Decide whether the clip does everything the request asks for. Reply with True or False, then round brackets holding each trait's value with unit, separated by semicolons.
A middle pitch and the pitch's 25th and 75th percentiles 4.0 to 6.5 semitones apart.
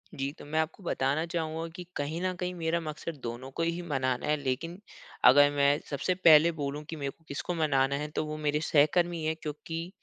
False (155 Hz; 2.7 semitones)